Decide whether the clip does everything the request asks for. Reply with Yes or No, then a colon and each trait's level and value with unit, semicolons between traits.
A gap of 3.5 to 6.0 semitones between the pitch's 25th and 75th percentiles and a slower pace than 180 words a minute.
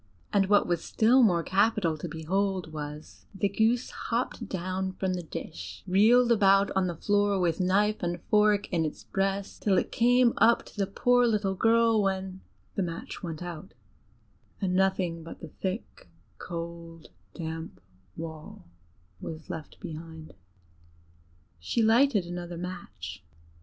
Yes: average, 3.8 semitones; average, 145 wpm